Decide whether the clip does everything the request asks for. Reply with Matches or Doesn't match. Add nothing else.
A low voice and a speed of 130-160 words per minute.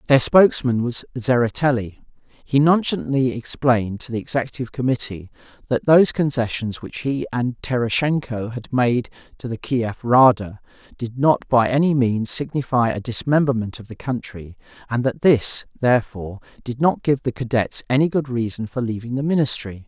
Matches